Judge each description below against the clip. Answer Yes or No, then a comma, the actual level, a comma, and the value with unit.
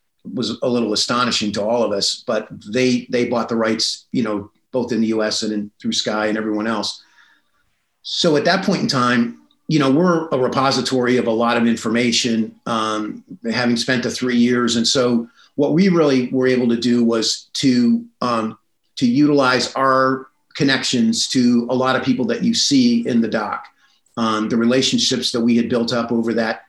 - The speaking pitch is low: Yes, low, 120 Hz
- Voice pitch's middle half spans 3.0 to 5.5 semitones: No, narrow, 2.6 semitones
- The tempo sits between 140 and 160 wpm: No, average, 195 wpm